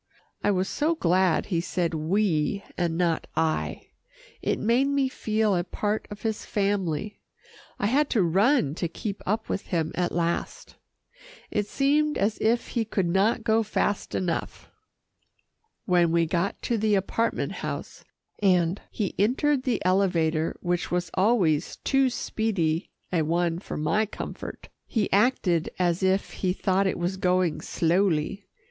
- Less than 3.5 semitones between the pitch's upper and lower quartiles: No, average, 4.1 semitones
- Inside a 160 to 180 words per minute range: No, average, 150 wpm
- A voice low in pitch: No, high, 190 Hz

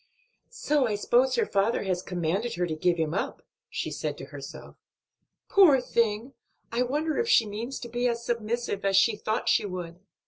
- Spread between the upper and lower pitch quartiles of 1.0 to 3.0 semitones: No, average, 4.4 semitones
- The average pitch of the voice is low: No, high, 230 Hz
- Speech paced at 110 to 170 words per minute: No, average, 185 wpm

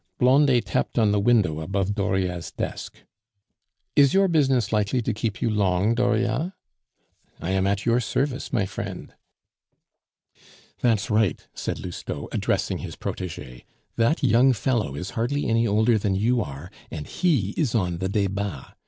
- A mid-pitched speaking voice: No, low, 110 Hz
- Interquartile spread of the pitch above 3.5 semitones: Yes, average, 4.3 semitones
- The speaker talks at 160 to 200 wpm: No, average, 150 wpm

